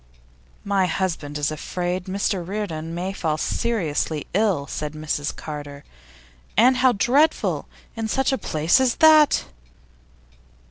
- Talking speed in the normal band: No, slow, 125 wpm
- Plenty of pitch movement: Yes, wide, 6.7 semitones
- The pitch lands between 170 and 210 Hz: Yes, medium, 185 Hz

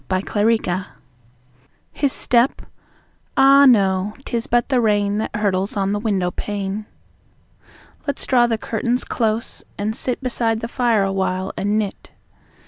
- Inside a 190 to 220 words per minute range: No, slow, 135 wpm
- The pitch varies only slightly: No, average, 3.3 semitones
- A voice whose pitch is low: No, high, 215 Hz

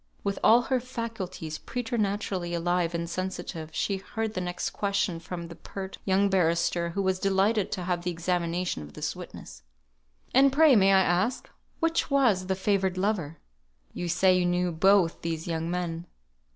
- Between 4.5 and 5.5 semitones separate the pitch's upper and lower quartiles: No, average, 2.8 semitones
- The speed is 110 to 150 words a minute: No, average, 165 wpm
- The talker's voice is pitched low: No, medium, 185 Hz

